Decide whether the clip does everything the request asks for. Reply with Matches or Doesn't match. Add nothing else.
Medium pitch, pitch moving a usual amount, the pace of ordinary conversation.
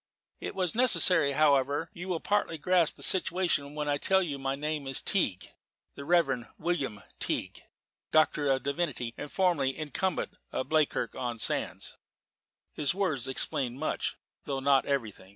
Matches